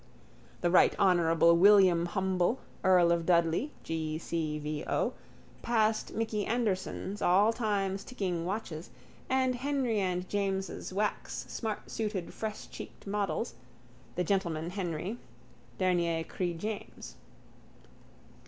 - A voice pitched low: No, high, 190 Hz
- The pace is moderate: No, slow, 105 wpm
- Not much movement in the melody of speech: No, average, 3.8 semitones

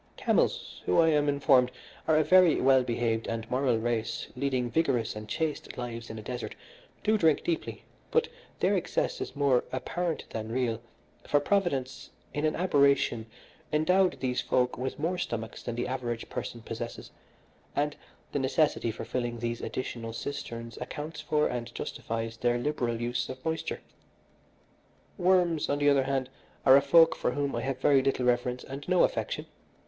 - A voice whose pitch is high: No, low, 130 Hz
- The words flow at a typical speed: Yes, average, 165 wpm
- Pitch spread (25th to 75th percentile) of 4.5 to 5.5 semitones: No, average, 4.1 semitones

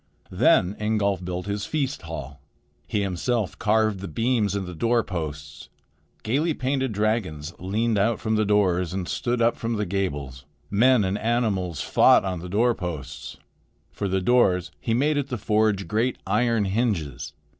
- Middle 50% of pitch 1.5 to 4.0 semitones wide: No, average, 4.4 semitones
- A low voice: Yes, low, 100 Hz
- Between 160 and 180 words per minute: Yes, average, 165 wpm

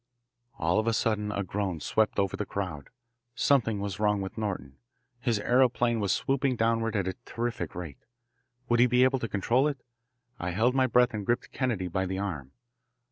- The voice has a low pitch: Yes, low, 105 Hz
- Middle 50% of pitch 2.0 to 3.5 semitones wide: No, average, 4.1 semitones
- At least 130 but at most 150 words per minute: No, average, 190 wpm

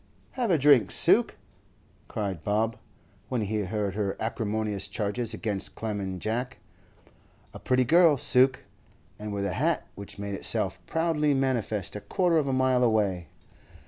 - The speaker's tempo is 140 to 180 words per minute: Yes, average, 150 wpm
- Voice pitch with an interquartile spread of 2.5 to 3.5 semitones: No, average, 4.4 semitones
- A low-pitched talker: Yes, low, 110 Hz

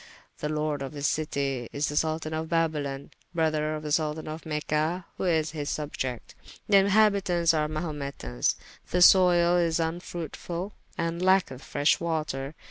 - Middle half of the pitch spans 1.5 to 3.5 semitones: Yes, narrow, 2.4 semitones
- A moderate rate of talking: Yes, average, 150 wpm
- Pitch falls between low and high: Yes, medium, 155 Hz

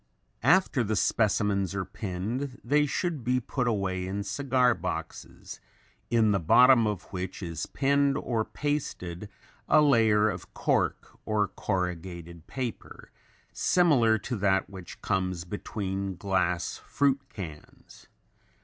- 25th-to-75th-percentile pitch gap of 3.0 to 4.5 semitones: No, wide, 5.4 semitones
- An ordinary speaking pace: No, slow, 120 wpm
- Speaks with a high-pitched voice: No, low, 105 Hz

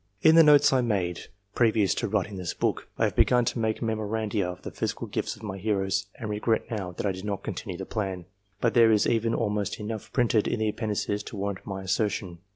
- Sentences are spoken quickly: Yes, fast, 225 wpm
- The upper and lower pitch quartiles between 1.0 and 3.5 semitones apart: Yes, narrow, 2.6 semitones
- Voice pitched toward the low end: Yes, low, 105 Hz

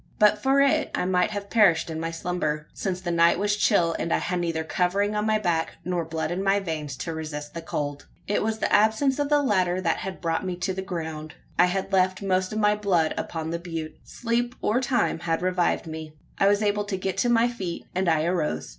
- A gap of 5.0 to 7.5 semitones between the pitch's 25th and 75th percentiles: No, average, 3.9 semitones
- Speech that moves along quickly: Yes, fast, 235 wpm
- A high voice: No, medium, 180 Hz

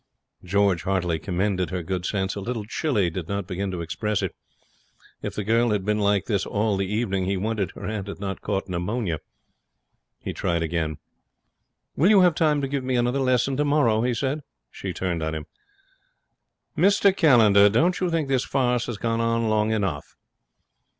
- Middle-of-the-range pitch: No, low, 105 Hz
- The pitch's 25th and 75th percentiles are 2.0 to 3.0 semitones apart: No, average, 4.8 semitones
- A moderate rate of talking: Yes, average, 185 wpm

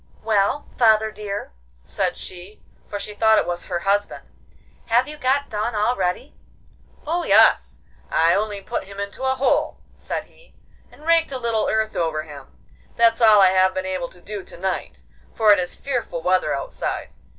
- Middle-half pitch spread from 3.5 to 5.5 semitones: Yes, average, 4.1 semitones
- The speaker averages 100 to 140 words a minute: No, average, 175 wpm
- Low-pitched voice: No, high, 210 Hz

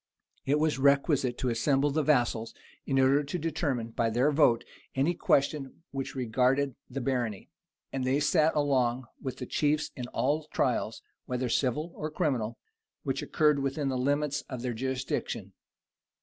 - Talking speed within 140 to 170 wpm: Yes, average, 155 wpm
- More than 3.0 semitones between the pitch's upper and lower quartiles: No, average, 2.7 semitones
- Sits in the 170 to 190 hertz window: No, low, 135 Hz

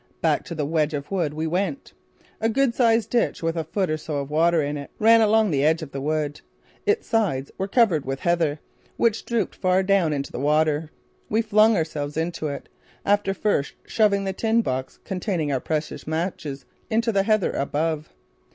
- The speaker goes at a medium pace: Yes, average, 195 wpm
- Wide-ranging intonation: Yes, wide, 6.0 semitones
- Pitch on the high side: No, medium, 165 Hz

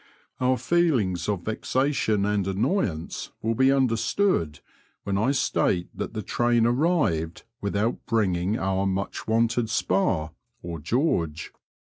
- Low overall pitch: Yes, low, 110 Hz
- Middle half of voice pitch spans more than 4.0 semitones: Yes, average, 5.1 semitones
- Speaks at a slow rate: Yes, slow, 125 wpm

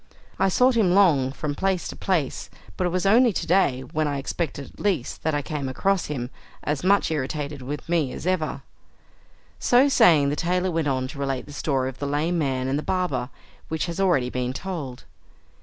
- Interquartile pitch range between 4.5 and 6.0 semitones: Yes, average, 5.0 semitones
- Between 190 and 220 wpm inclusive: Yes, fast, 205 wpm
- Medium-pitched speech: Yes, medium, 150 Hz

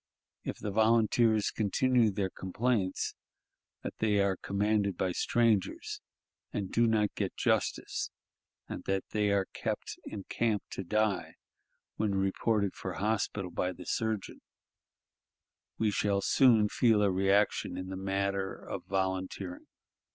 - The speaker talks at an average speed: No, slow, 130 wpm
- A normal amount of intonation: No, narrow, 2.2 semitones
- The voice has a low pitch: Yes, low, 100 Hz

